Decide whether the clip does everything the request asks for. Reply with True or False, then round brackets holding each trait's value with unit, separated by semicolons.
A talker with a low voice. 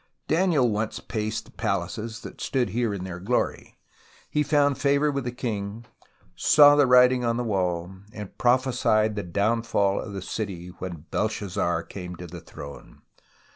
True (110 Hz)